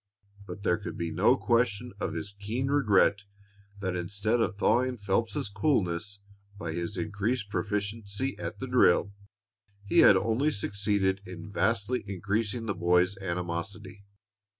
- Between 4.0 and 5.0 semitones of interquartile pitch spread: No, average, 3.2 semitones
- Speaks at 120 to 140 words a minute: Yes, slow, 135 wpm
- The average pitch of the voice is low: Yes, low, 100 Hz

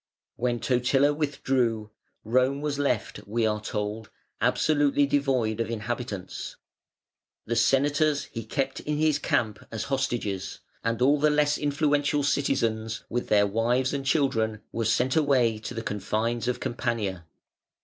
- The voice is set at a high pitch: No, low, 125 Hz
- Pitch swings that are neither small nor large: Yes, average, 4.3 semitones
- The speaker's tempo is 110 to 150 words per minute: Yes, average, 140 wpm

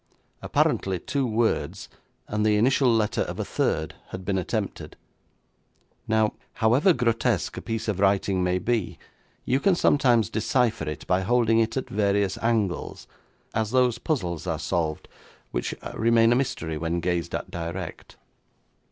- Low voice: Yes, low, 110 Hz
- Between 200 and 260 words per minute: No, average, 145 wpm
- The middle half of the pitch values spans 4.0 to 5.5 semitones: Yes, average, 4.5 semitones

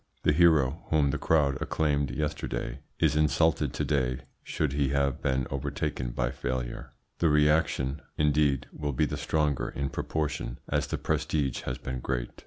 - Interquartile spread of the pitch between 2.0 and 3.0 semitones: Yes, narrow, 2.5 semitones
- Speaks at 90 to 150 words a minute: No, average, 160 wpm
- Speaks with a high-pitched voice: No, very low, 70 Hz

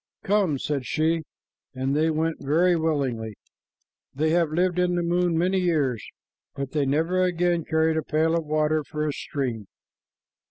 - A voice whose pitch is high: No, medium, 160 Hz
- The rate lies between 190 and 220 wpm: No, average, 160 wpm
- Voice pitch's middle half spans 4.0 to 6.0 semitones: No, average, 3.1 semitones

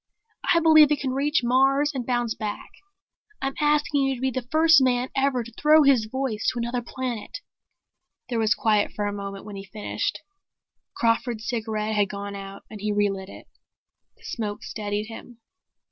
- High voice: Yes, high, 235 Hz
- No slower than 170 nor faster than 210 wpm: Yes, average, 175 wpm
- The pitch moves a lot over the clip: No, average, 4.3 semitones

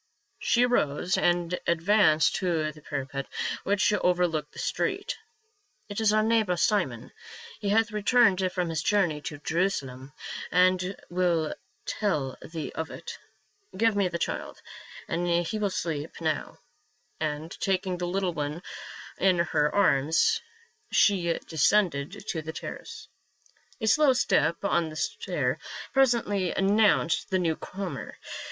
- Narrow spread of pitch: No, average, 4.4 semitones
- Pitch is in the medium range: Yes, medium, 180 Hz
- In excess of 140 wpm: No, slow, 135 wpm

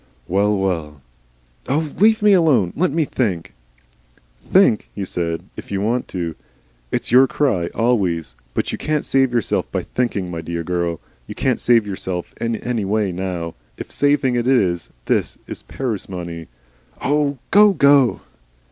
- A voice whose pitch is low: Yes, low, 105 Hz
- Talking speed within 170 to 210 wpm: No, average, 160 wpm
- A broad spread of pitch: Yes, wide, 7.5 semitones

